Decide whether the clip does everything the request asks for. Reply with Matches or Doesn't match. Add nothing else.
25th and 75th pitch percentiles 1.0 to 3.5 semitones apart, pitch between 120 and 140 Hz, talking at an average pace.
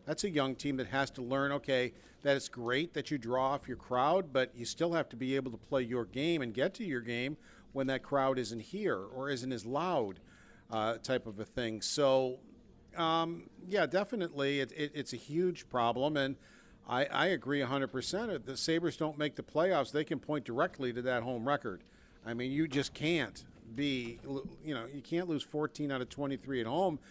Doesn't match